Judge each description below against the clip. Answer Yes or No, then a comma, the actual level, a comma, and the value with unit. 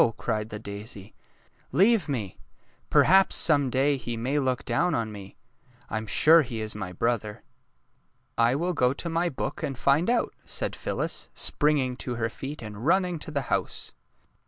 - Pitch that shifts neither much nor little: No, wide, 5.9 semitones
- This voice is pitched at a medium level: No, low, 130 Hz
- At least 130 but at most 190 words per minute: Yes, average, 180 wpm